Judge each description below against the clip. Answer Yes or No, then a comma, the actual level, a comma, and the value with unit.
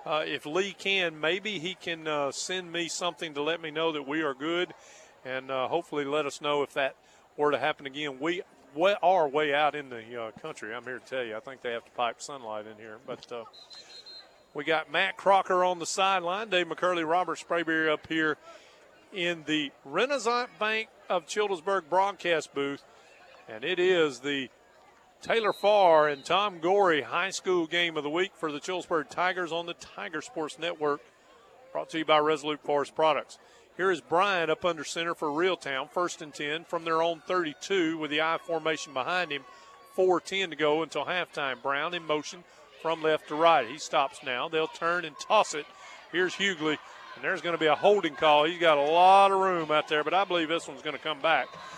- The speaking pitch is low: No, medium, 165 Hz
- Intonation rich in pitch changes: No, average, 3.3 semitones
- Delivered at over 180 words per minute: Yes, fast, 205 wpm